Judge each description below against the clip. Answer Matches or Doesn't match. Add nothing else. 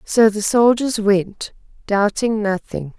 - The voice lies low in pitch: Doesn't match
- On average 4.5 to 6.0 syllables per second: Doesn't match